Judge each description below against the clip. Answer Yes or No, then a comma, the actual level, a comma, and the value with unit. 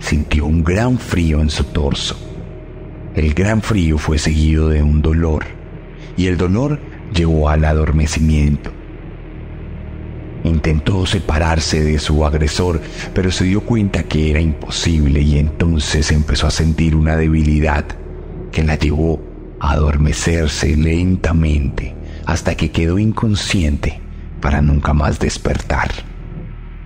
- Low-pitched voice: Yes, very low, 80 Hz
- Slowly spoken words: Yes, slow, 120 wpm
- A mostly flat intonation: Yes, narrow, 2.3 semitones